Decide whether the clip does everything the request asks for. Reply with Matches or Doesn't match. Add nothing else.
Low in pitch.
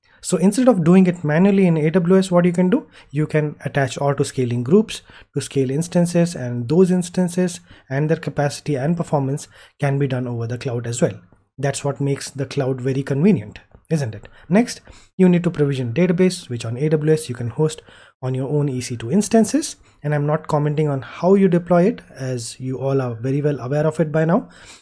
Doesn't match